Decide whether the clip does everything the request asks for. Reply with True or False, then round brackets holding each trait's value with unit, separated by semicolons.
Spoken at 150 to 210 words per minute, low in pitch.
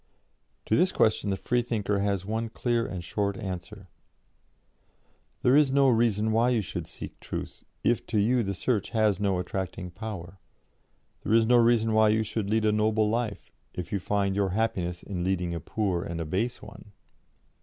True (180 wpm; 105 Hz)